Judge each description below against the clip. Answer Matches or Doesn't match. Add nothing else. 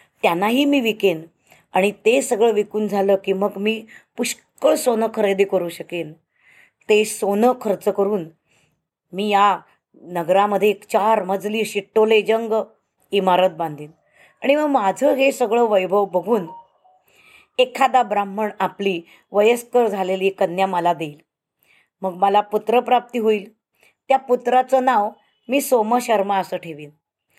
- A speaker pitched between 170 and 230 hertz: Matches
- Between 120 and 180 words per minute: Matches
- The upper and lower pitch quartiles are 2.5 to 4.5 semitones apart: Matches